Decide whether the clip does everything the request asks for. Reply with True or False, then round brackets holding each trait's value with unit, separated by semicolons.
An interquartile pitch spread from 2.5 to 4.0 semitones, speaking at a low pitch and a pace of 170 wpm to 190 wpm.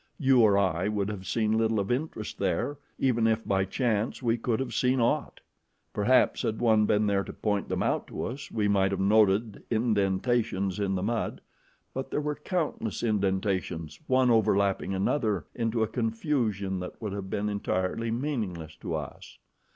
True (3.3 semitones; 110 Hz; 175 wpm)